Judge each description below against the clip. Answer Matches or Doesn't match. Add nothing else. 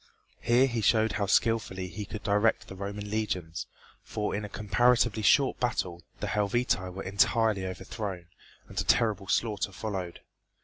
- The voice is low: Matches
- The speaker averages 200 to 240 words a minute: Doesn't match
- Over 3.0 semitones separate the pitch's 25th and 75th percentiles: Doesn't match